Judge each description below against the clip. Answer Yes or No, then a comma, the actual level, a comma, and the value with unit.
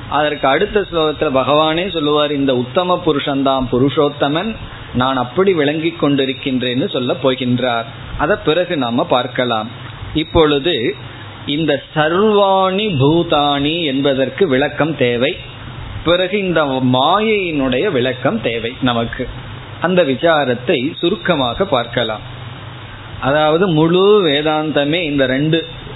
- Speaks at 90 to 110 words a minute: Yes, average, 95 wpm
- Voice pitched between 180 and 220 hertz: No, medium, 140 Hz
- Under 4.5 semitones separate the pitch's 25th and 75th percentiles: Yes, average, 3.9 semitones